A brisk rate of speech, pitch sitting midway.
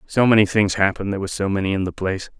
No: fast, 250 wpm; low, 100 Hz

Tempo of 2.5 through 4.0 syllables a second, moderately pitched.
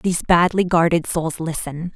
No: 4.7 syllables/s; medium, 170 Hz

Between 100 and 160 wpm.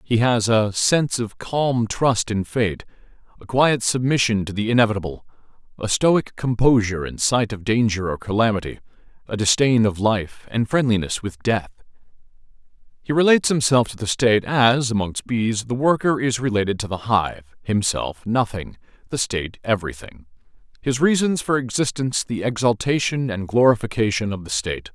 Yes: average, 155 wpm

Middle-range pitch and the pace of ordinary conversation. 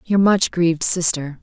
Yes: medium, 175 Hz; average, 170 wpm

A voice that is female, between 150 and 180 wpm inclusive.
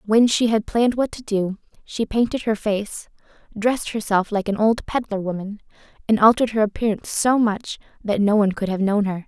No: female; average, 200 wpm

